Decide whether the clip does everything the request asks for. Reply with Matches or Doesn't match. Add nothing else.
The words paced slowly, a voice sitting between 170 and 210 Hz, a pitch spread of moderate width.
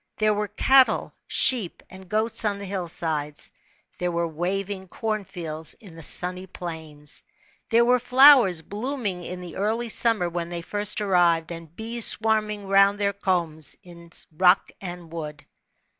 Doesn't match